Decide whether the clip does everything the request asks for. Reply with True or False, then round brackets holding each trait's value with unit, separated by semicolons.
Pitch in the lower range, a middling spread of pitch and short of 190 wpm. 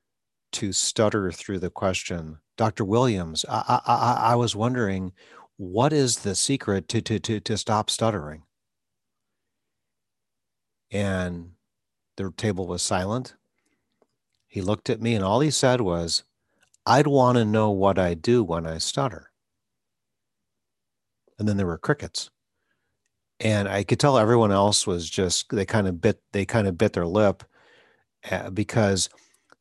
True (100 Hz; 3.7 semitones; 140 wpm)